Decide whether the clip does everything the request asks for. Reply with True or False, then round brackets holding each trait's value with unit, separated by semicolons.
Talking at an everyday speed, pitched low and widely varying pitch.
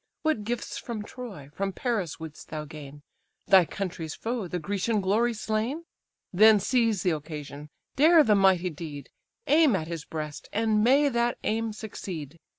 False (155 wpm; 200 Hz; 6.2 semitones)